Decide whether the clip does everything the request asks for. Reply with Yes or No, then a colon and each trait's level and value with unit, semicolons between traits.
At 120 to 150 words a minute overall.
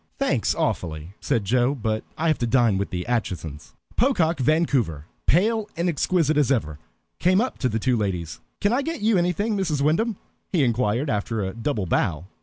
No: average, 185 wpm